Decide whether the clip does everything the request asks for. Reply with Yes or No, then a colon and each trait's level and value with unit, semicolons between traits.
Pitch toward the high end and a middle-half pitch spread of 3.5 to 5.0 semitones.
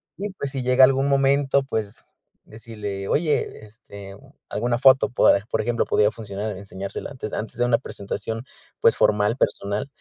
No: low, 115 Hz; average, 4.6 semitones